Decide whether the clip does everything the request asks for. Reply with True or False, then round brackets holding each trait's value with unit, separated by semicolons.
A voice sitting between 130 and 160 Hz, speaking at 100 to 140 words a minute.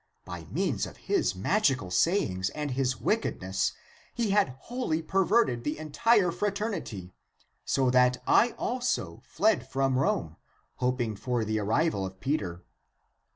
True (135 Hz; 135 wpm)